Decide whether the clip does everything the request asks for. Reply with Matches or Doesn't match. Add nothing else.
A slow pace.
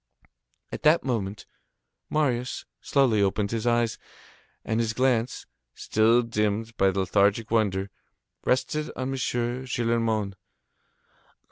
Matches